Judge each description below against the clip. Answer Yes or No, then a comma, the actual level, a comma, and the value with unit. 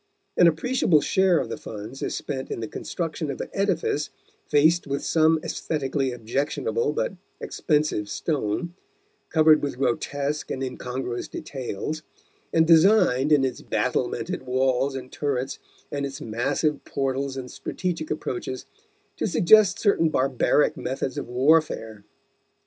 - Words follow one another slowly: Yes, slow, 130 wpm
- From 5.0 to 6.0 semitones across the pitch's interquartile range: No, average, 3.8 semitones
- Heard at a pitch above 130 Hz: Yes, medium, 140 Hz